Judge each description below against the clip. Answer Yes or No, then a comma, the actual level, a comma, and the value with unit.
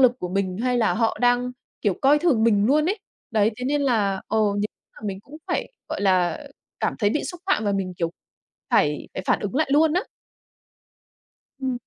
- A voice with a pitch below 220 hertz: No, high, 225 Hz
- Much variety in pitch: Yes, wide, 5.7 semitones